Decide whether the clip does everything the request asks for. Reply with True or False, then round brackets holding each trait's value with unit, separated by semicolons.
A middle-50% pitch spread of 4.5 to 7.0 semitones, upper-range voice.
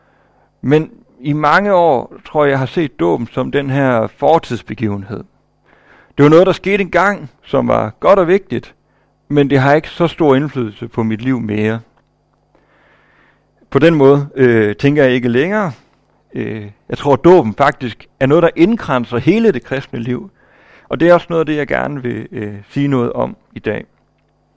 False (5.0 semitones; 140 Hz)